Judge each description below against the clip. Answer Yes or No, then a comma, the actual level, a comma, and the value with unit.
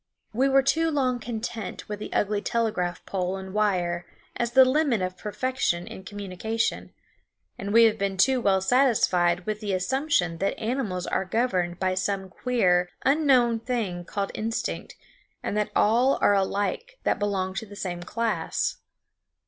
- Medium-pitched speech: No, high, 210 Hz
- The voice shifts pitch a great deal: No, average, 4.5 semitones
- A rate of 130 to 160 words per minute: Yes, average, 155 wpm